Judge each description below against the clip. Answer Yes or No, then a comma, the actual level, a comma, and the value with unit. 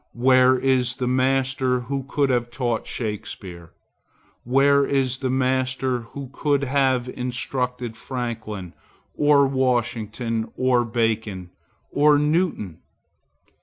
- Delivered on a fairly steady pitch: Yes, narrow, 2.3 semitones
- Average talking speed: No, slow, 105 wpm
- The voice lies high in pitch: No, low, 125 Hz